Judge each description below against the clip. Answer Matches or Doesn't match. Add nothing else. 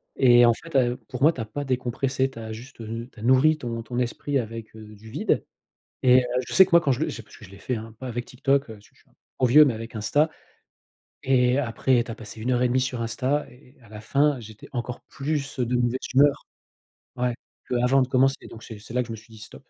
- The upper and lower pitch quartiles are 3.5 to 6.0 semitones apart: Doesn't match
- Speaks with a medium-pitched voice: Doesn't match